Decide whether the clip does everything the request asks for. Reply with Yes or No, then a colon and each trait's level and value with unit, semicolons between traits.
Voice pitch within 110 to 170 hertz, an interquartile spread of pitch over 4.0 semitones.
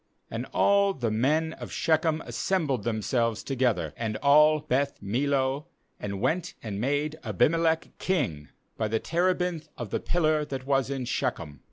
Yes: medium, 140 Hz; average, 5.1 semitones